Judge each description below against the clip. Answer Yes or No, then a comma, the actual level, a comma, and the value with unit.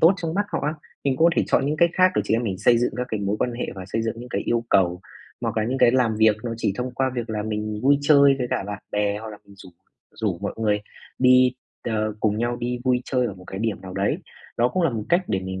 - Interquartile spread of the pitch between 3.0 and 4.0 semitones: Yes, average, 3.7 semitones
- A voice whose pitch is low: Yes, low, 115 Hz